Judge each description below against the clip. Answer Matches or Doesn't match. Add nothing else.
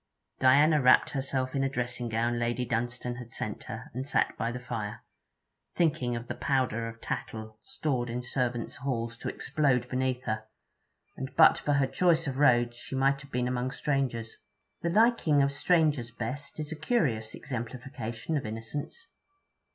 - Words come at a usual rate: Matches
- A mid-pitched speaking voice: Doesn't match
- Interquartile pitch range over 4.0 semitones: Doesn't match